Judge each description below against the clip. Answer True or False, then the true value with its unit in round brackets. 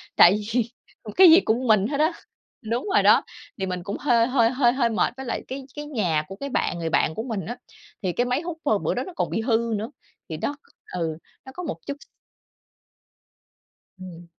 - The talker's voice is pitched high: True (230 Hz)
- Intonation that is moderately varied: False (6.0 semitones)